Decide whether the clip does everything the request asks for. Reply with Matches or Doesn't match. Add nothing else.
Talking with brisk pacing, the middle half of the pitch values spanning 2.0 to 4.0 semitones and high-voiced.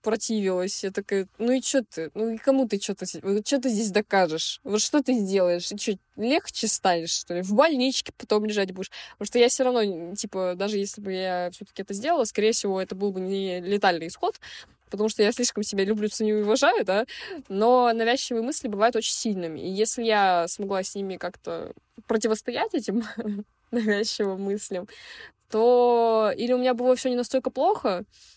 Matches